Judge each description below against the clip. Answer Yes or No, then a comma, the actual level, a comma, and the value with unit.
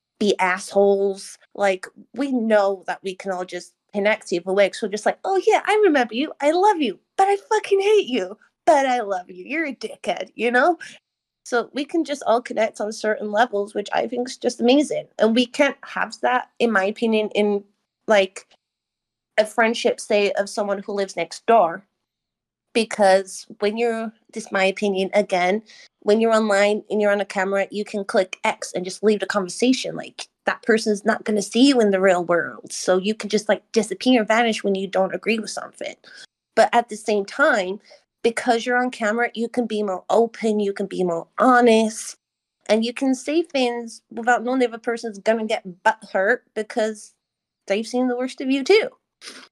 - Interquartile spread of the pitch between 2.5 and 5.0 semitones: Yes, average, 3.5 semitones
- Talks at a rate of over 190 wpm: Yes, average, 200 wpm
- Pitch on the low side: No, high, 215 Hz